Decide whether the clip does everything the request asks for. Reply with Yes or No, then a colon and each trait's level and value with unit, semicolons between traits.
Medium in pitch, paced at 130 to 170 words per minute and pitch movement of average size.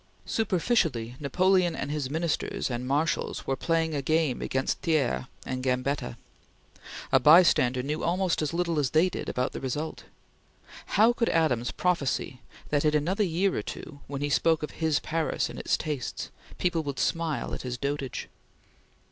Yes: medium, 150 Hz; average, 165 wpm; average, 4.0 semitones